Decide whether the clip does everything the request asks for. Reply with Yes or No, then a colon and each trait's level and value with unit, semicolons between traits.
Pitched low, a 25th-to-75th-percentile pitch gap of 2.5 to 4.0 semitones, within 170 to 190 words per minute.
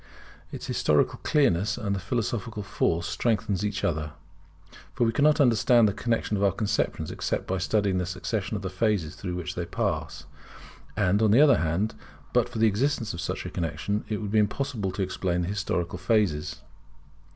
Yes: low, 100 Hz; average, 3.7 semitones; average, 185 wpm